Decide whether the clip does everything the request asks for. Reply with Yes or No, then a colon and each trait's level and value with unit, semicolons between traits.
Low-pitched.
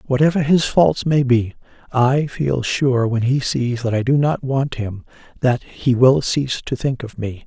Yes: low, 130 Hz